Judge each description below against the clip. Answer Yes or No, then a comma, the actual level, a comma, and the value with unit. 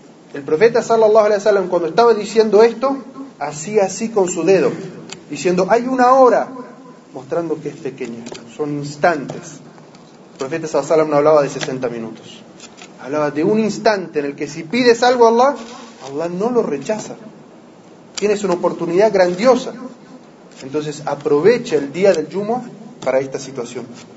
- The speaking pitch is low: No, medium, 185 Hz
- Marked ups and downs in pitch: Yes, wide, 7.5 semitones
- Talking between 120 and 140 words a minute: No, average, 150 wpm